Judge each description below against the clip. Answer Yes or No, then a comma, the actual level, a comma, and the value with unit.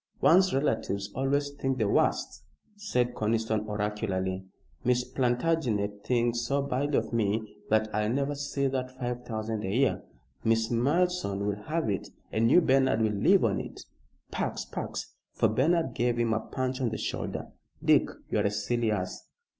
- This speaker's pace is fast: No, average, 160 wpm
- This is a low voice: Yes, low, 120 Hz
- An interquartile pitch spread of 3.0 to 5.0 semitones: Yes, average, 4.1 semitones